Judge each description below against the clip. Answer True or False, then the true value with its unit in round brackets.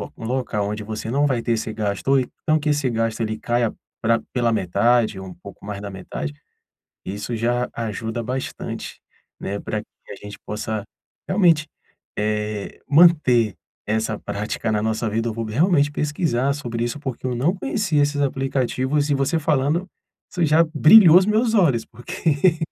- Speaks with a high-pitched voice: False (120 Hz)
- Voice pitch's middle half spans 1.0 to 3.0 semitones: False (5.3 semitones)